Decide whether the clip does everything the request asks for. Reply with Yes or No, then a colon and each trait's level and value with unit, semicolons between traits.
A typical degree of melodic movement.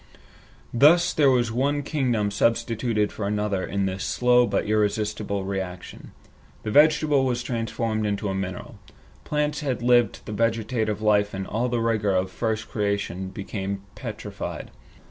Yes: average, 3.3 semitones